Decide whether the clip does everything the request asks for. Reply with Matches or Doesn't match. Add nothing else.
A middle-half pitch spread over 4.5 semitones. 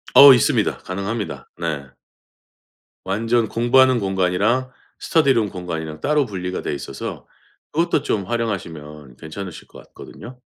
Matches